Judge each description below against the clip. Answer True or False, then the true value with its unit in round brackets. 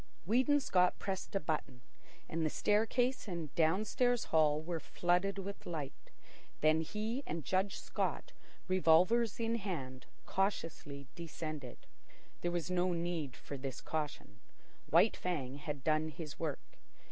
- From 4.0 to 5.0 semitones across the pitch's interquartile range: True (4.3 semitones)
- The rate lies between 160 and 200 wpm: False (135 wpm)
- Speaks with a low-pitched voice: False (170 Hz)